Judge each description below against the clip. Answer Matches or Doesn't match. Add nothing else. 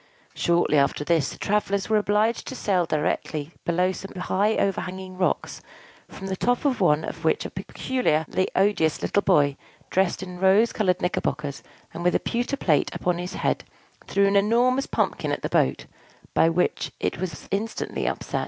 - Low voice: Doesn't match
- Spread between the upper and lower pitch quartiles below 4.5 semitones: Matches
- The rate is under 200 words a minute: Matches